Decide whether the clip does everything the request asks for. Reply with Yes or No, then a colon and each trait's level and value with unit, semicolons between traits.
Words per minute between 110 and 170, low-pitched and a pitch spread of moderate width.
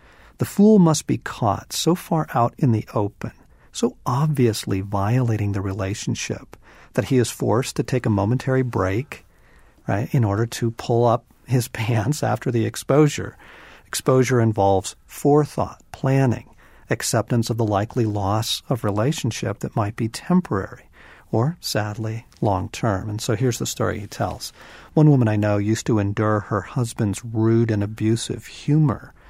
Yes: average, 155 wpm; low, 115 Hz; average, 3.7 semitones